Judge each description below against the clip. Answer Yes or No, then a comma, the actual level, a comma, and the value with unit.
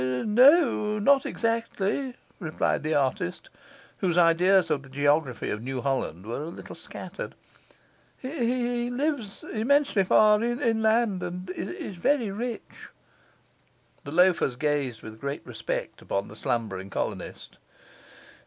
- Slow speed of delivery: Yes, slow, 120 wpm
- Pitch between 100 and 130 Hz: No, medium, 185 Hz